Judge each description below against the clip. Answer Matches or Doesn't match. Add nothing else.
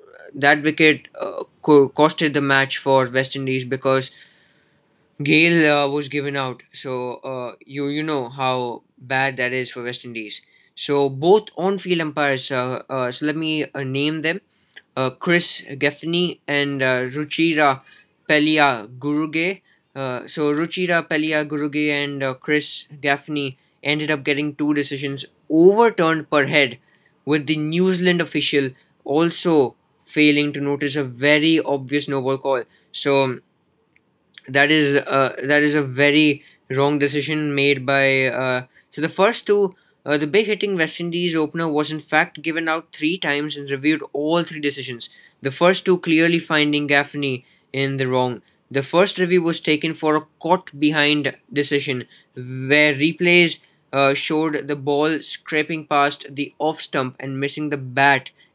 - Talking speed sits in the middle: Matches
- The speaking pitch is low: Doesn't match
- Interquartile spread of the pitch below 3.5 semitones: Matches